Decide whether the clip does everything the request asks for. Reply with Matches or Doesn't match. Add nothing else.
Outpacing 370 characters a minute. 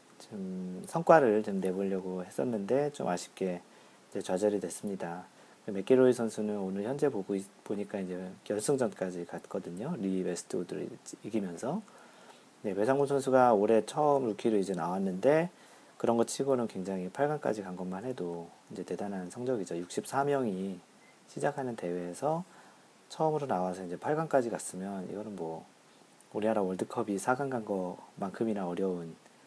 Doesn't match